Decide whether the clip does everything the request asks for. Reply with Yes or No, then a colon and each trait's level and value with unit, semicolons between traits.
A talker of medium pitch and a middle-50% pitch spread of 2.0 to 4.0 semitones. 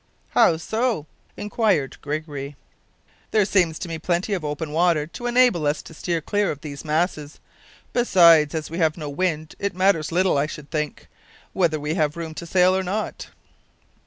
Yes: medium, 165 Hz; average, 3.6 semitones